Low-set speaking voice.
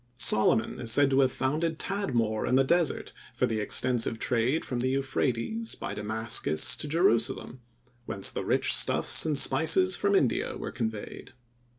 Yes: low, 130 Hz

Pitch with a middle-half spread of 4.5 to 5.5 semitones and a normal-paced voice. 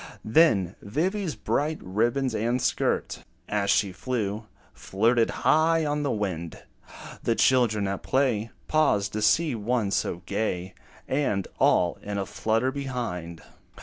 No: average, 5.2 semitones; slow, 130 wpm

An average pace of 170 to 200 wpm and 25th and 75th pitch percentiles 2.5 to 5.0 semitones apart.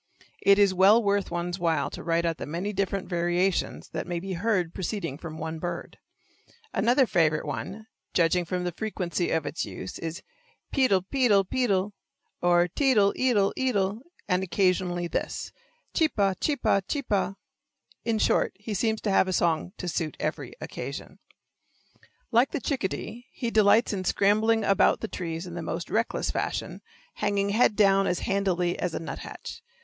Yes: average, 180 wpm; average, 3.5 semitones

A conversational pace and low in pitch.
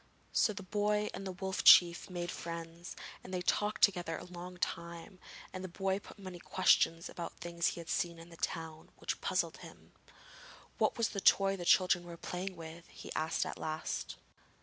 No: average, 190 wpm; medium, 175 Hz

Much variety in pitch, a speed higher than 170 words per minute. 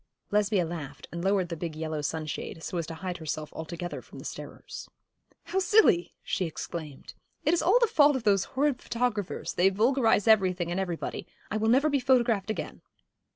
Yes: wide, 6.5 semitones; average, 185 wpm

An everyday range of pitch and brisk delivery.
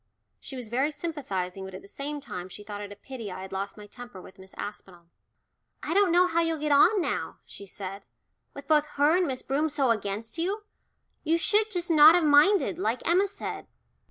No: wide, 8.4 semitones; fast, 215 wpm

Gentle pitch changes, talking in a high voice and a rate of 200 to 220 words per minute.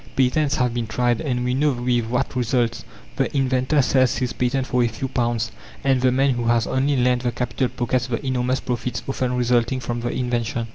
No: narrow, 1.4 semitones; low, 125 Hz; fast, 205 wpm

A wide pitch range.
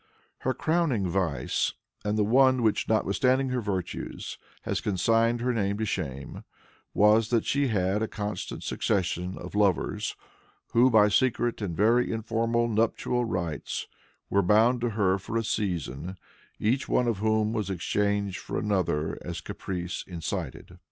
No: average, 3.5 semitones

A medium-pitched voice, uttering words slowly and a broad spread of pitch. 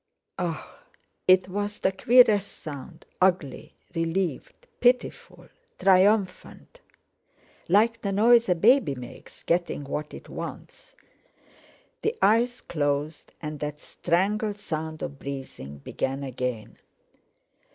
Yes: medium, 180 Hz; slow, 100 wpm; wide, 6.0 semitones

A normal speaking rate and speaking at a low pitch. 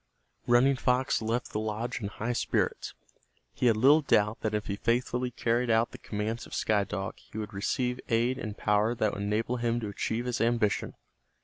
Yes: average, 195 wpm; low, 115 Hz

